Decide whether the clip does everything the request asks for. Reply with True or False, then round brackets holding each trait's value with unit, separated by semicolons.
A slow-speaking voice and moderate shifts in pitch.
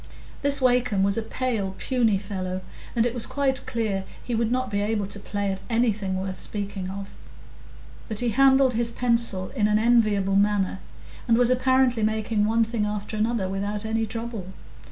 False (175 wpm; 3.1 semitones)